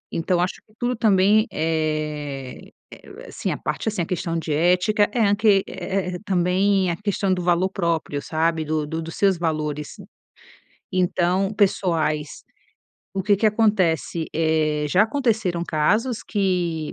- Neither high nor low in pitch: Yes, medium, 180 Hz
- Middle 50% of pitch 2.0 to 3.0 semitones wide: No, average, 3.8 semitones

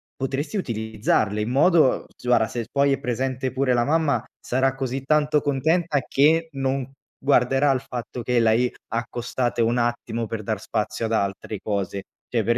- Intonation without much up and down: No, average, 3.2 semitones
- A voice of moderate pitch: No, low, 125 Hz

